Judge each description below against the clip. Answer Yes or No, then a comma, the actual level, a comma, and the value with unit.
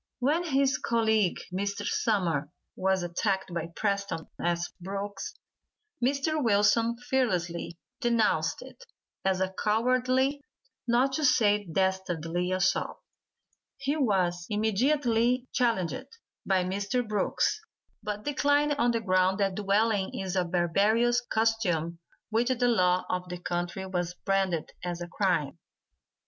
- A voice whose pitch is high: Yes, high, 205 Hz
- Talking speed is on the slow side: Yes, slow, 120 wpm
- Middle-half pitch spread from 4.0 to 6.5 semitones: Yes, average, 4.8 semitones